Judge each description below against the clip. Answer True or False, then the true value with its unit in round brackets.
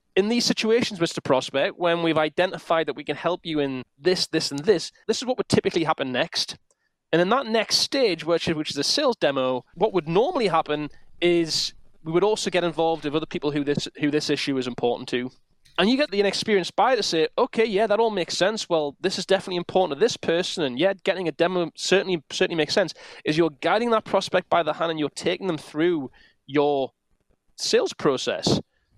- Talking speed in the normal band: False (215 wpm)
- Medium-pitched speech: True (170 Hz)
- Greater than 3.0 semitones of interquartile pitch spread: True (4.6 semitones)